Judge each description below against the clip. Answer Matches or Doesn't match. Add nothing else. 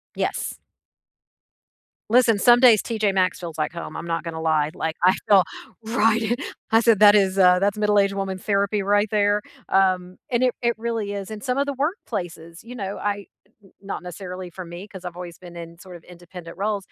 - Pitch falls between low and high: Doesn't match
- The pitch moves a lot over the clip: Doesn't match